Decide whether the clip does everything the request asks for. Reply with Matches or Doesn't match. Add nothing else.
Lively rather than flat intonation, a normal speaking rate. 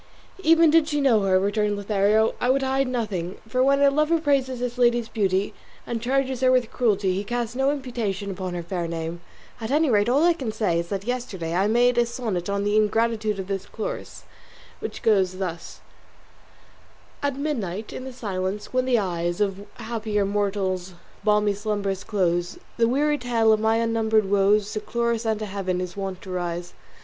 Doesn't match